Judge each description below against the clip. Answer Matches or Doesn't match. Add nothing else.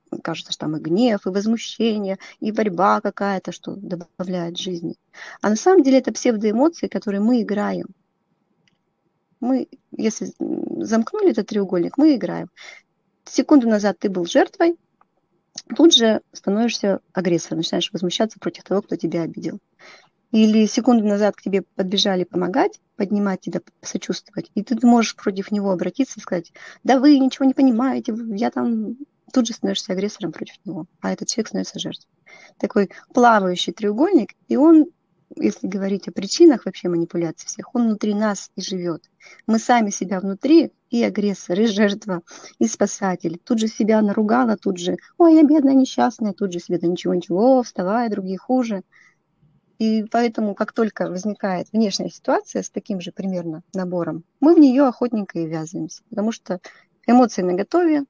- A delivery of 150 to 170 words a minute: Matches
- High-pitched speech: Matches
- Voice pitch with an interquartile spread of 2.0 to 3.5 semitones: Doesn't match